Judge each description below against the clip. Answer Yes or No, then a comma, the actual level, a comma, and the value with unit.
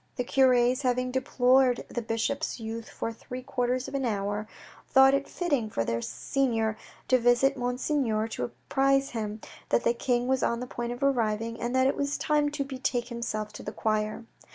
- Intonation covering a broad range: No, average, 3.0 semitones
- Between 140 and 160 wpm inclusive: No, average, 185 wpm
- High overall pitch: Yes, high, 245 Hz